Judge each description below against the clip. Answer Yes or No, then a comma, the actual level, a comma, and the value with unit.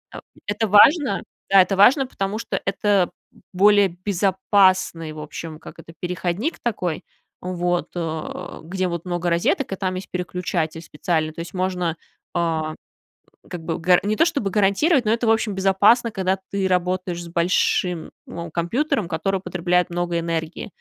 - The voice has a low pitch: No, medium, 185 Hz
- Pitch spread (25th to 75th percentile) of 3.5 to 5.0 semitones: No, average, 2.8 semitones